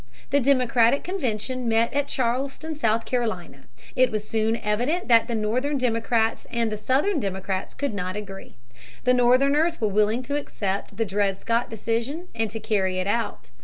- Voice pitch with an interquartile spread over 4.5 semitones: No, average, 3.5 semitones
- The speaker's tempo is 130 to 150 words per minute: No, average, 165 wpm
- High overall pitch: Yes, high, 230 Hz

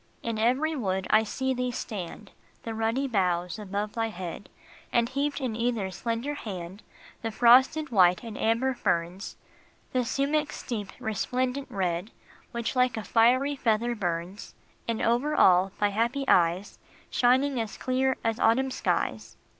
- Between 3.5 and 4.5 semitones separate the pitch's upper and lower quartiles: Yes, average, 4.2 semitones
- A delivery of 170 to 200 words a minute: No, average, 150 wpm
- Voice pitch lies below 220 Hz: No, high, 230 Hz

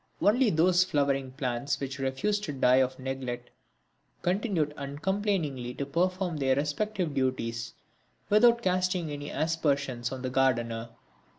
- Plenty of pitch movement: Yes, wide, 5.7 semitones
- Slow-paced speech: Yes, slow, 125 wpm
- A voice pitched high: No, medium, 145 Hz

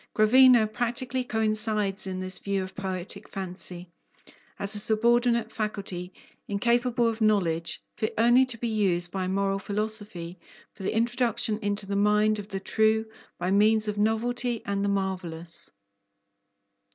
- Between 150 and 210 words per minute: No, average, 140 wpm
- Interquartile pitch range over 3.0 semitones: No, average, 2.7 semitones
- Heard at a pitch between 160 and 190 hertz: No, high, 210 Hz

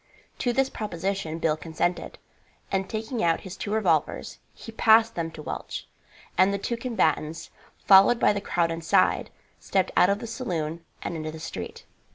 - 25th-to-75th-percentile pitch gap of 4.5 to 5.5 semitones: Yes, average, 5.0 semitones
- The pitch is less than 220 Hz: Yes, high, 190 Hz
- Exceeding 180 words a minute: No, average, 170 wpm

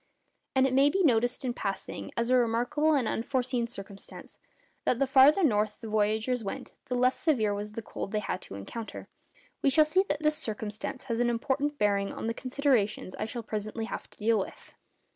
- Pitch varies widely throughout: No, average, 3.9 semitones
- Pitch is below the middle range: No, high, 235 Hz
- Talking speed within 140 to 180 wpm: No, average, 200 wpm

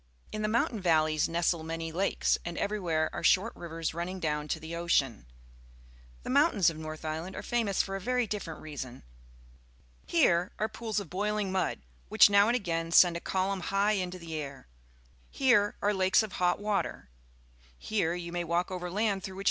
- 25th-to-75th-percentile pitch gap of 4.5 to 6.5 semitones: No, average, 3.8 semitones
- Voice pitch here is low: No, medium, 180 Hz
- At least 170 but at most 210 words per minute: Yes, average, 180 wpm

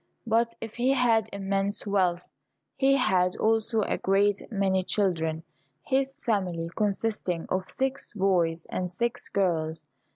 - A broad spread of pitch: No, average, 3.9 semitones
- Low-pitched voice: No, high, 200 Hz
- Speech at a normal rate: No, slow, 130 wpm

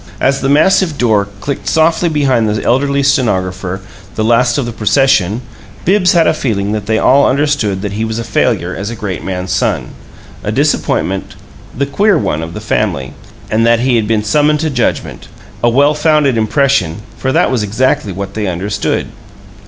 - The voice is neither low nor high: No, low, 115 Hz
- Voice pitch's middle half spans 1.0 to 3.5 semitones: No, wide, 5.4 semitones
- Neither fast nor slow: Yes, average, 185 wpm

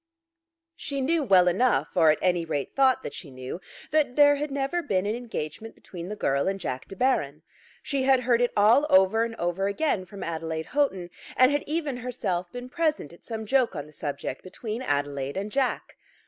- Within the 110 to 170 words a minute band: No, average, 200 wpm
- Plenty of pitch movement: Yes, wide, 7.4 semitones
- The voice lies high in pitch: Yes, high, 210 Hz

